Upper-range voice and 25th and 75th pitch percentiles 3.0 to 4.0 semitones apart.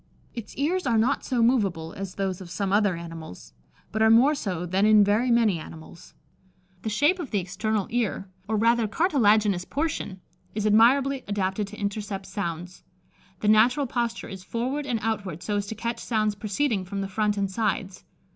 Yes: high, 210 Hz; average, 3.4 semitones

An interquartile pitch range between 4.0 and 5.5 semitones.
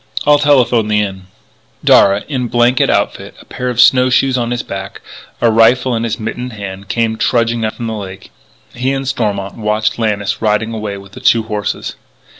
No: average, 2.9 semitones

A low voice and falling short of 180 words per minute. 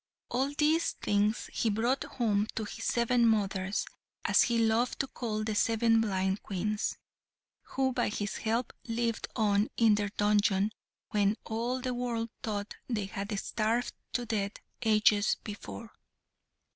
No: high, 220 Hz; average, 145 wpm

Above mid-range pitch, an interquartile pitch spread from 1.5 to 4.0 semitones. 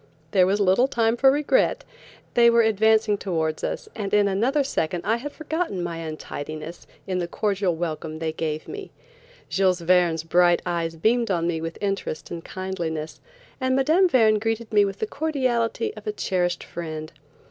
No: high, 195 Hz; wide, 5.6 semitones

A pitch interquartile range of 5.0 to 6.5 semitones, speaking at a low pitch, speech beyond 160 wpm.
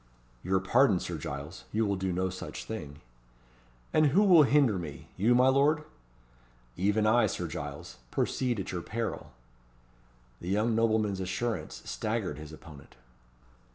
No: wide, 5.4 semitones; low, 100 Hz; average, 145 wpm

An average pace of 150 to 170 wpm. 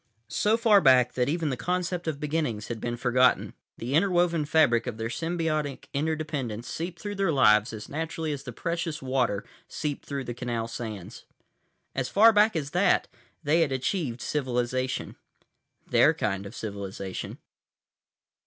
Yes: average, 155 wpm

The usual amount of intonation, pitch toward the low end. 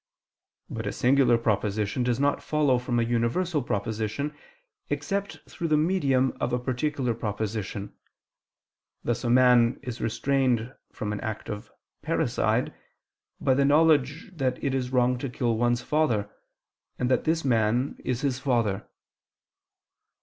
Yes: average, 3.3 semitones; low, 125 Hz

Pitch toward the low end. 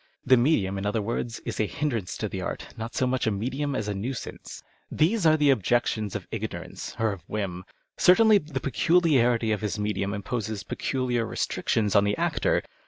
Yes: low, 115 Hz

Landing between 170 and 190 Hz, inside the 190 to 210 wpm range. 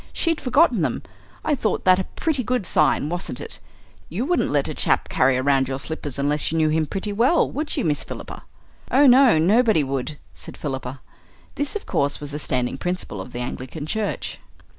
No: medium, 160 Hz; average, 195 wpm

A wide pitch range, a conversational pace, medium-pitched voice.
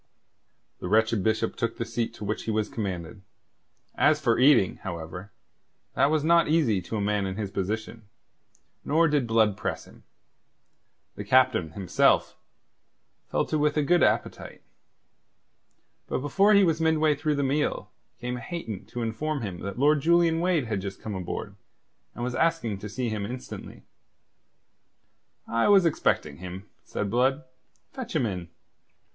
No: wide, 6.9 semitones; average, 155 wpm; low, 115 Hz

